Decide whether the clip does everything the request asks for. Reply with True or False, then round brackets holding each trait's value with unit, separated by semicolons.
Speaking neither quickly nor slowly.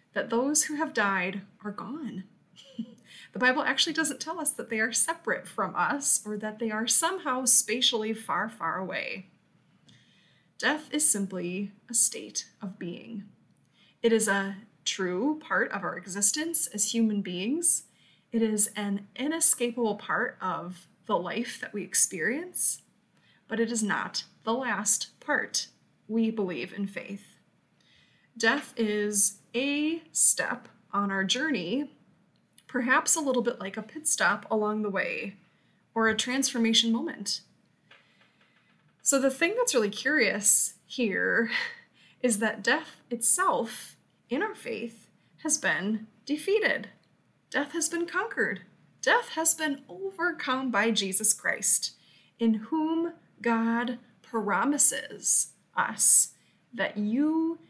False (130 wpm)